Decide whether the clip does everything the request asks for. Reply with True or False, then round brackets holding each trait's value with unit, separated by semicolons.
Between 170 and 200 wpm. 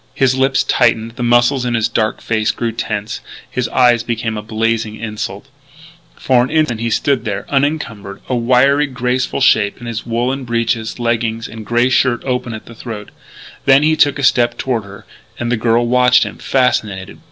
True (185 wpm)